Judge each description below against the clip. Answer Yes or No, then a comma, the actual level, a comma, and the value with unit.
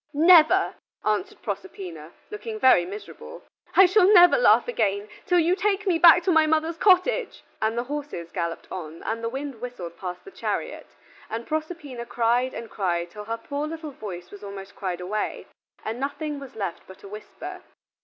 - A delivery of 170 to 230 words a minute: Yes, average, 175 wpm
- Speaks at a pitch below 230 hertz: No, very high, 250 Hz